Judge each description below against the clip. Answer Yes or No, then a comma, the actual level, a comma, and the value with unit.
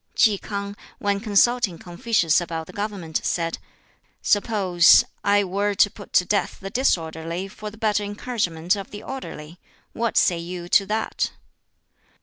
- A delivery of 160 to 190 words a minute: No, average, 145 wpm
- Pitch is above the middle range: Yes, high, 200 Hz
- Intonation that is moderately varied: Yes, average, 3.4 semitones